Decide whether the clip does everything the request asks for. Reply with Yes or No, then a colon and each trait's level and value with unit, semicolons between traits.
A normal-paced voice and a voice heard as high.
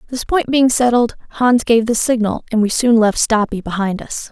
No: fast, 210 wpm; high, 230 Hz